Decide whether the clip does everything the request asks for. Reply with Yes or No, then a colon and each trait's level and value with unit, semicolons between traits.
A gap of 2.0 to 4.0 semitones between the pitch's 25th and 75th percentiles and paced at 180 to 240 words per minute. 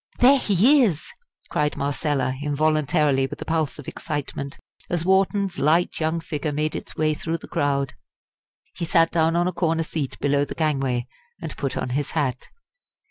No: average, 2.8 semitones; average, 170 wpm